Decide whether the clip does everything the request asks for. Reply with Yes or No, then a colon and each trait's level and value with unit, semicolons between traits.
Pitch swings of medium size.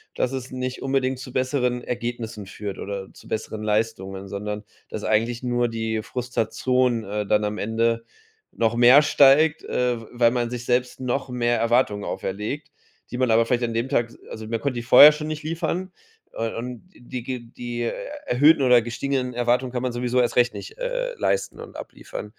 No: narrow, 2.2 semitones